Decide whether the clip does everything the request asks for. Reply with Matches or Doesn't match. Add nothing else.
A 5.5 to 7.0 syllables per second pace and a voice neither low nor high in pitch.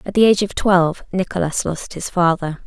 Matches